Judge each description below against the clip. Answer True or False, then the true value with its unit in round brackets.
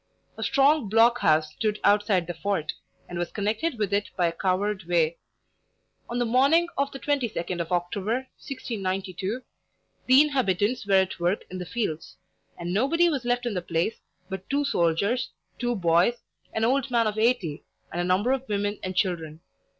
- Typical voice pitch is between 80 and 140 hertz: False (205 Hz)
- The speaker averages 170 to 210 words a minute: True (180 wpm)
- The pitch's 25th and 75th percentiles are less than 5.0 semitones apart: False (5.5 semitones)